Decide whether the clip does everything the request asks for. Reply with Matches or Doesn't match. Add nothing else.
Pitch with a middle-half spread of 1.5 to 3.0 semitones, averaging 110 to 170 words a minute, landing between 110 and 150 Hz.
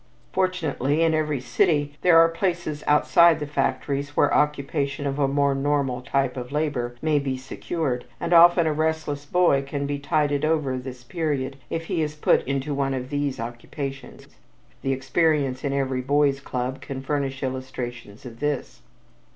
Matches